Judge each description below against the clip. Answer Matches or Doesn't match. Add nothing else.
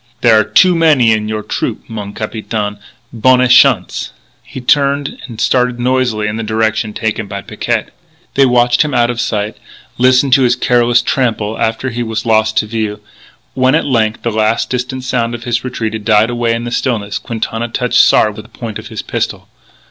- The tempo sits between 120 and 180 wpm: Doesn't match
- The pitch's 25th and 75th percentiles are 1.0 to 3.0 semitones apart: Matches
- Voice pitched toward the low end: Matches